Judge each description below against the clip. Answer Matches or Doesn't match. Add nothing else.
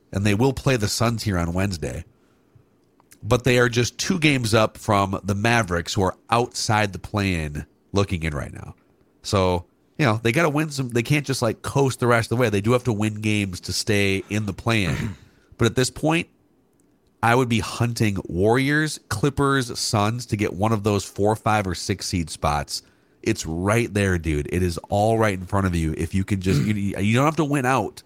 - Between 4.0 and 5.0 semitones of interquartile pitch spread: Matches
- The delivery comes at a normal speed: Doesn't match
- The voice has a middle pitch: Doesn't match